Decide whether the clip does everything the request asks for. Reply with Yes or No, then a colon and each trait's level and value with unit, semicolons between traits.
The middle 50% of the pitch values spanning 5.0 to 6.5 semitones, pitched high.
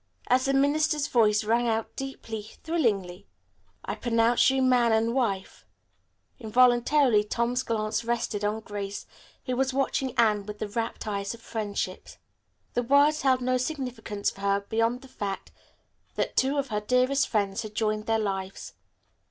No: average, 3.5 semitones; high, 230 Hz